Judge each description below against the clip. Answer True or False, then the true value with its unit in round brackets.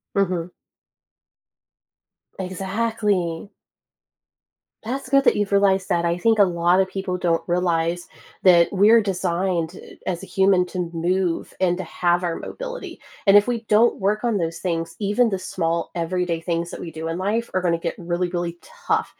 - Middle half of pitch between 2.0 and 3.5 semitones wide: True (2.7 semitones)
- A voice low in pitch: False (180 Hz)